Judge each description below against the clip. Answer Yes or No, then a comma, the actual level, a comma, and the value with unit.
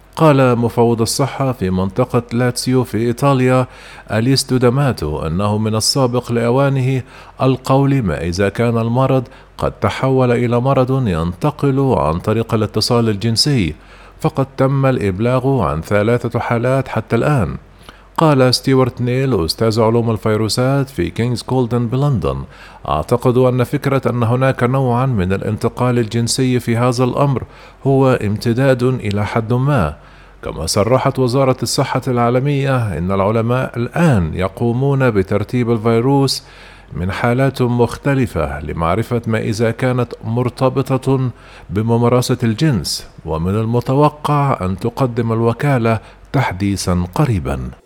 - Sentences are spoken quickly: No, average, 115 wpm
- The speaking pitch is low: Yes, low, 120 Hz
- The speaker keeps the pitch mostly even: No, average, 3.2 semitones